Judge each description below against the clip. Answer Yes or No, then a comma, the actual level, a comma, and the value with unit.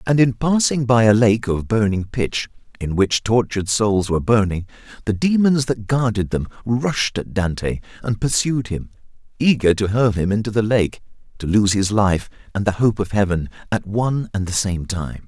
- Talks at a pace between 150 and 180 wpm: No, average, 190 wpm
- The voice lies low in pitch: Yes, low, 110 Hz